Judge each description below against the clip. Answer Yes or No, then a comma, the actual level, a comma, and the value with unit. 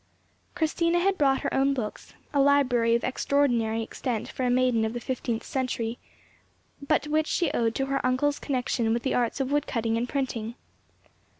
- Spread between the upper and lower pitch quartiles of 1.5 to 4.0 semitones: Yes, average, 3.4 semitones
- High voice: Yes, very high, 255 Hz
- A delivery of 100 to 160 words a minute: No, average, 175 wpm